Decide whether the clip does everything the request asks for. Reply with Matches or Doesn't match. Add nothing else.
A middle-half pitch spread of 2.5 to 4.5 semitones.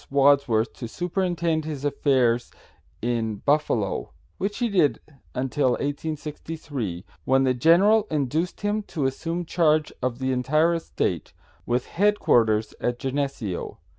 Doesn't match